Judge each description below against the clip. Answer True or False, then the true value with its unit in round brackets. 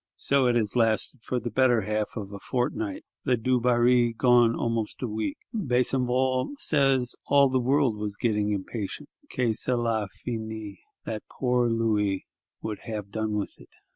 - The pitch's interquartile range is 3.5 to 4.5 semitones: False (2.9 semitones)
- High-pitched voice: False (120 Hz)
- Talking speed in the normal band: True (155 wpm)